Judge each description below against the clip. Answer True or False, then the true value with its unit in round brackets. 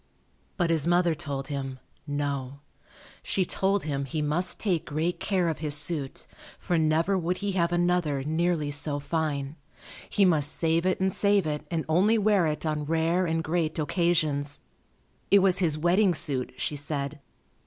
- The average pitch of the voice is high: False (160 Hz)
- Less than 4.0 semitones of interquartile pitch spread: True (3.3 semitones)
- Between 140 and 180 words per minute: True (165 wpm)